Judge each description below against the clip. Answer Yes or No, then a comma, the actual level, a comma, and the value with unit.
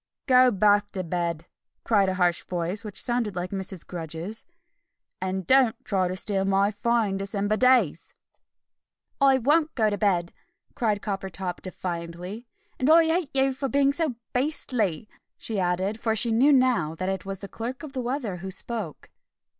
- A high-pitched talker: Yes, high, 205 Hz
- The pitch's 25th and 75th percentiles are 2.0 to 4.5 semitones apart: No, average, 5.3 semitones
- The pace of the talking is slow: No, average, 165 wpm